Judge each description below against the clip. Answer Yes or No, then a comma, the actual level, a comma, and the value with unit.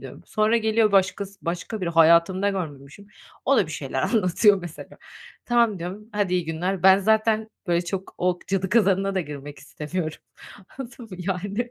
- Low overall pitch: No, high, 190 Hz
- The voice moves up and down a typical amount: Yes, average, 3.5 semitones